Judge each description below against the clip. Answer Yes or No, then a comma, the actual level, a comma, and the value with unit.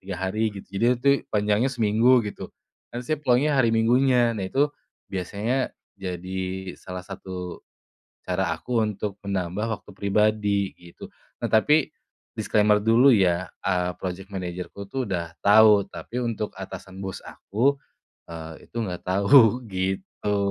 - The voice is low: Yes, low, 100 Hz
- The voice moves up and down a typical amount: Yes, average, 3.7 semitones